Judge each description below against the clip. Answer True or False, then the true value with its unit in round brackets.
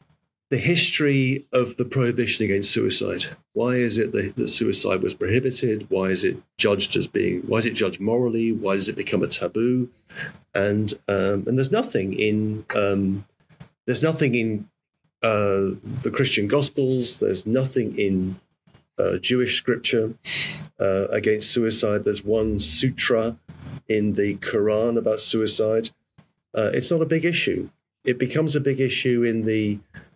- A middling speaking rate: True (150 wpm)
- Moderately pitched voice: False (115 Hz)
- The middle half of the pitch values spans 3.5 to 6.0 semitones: True (4.0 semitones)